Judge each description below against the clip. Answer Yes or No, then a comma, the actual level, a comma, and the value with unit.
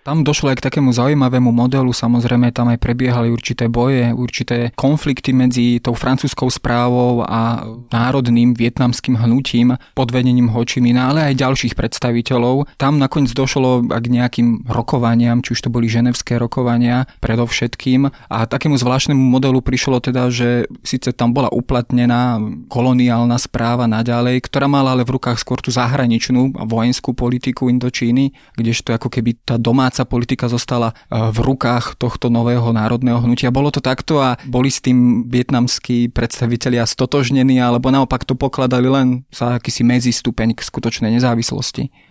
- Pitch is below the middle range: Yes, low, 125 Hz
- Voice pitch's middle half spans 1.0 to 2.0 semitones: Yes, narrow, 1.5 semitones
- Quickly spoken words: No, average, 145 wpm